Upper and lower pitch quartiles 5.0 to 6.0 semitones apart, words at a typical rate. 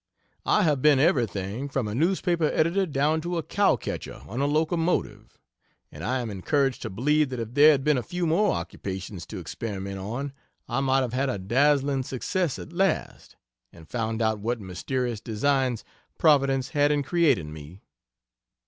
Yes: wide, 5.4 semitones; average, 175 wpm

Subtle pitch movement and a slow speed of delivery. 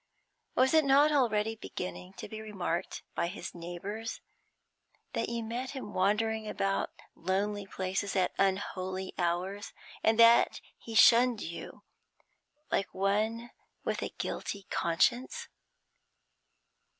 No: average, 3.4 semitones; slow, 115 wpm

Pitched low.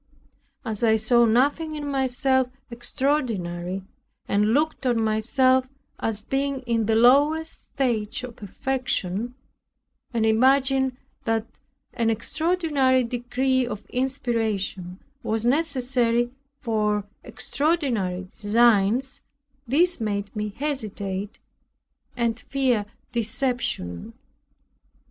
No: high, 240 Hz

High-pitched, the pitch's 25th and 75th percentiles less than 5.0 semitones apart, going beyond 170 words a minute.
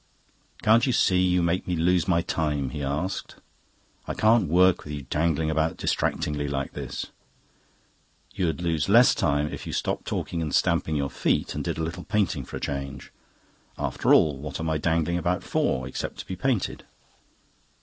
No: very low, 80 Hz; average, 3.6 semitones; average, 180 wpm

